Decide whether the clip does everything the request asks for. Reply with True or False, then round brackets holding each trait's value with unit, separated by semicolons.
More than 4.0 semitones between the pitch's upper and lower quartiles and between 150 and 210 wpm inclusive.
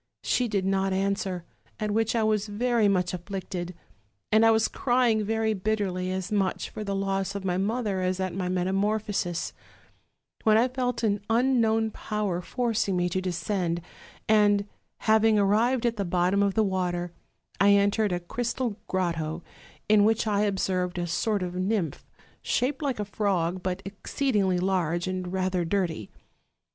False (3.0 semitones; 160 wpm)